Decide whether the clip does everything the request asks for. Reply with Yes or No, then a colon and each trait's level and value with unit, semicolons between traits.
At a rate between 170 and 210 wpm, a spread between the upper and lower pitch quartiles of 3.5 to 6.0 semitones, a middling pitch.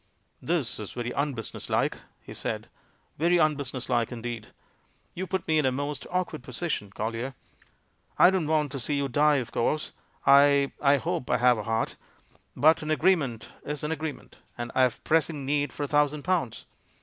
Yes: average, 190 wpm; average, 3.9 semitones; medium, 145 Hz